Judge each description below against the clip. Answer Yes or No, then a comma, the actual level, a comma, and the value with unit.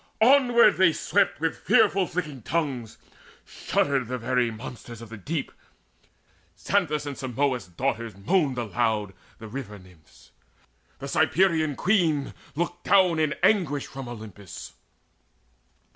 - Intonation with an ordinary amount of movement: No, wide, 6.3 semitones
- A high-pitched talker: No, low, 135 Hz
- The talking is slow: Yes, slow, 120 wpm